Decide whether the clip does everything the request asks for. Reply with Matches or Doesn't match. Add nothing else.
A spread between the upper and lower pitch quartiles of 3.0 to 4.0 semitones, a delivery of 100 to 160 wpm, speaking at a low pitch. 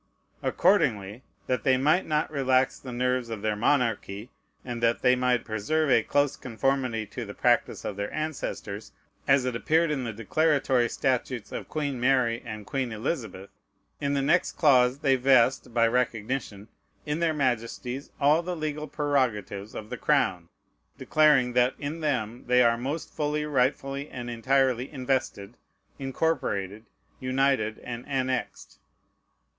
Matches